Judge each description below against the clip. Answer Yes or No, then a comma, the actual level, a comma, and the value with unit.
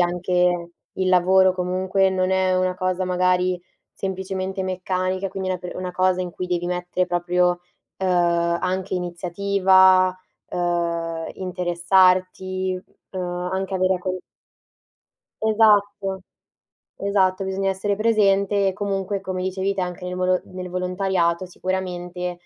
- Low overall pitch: No, medium, 185 Hz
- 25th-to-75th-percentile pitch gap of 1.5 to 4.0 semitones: No, narrow, 1.0 semitones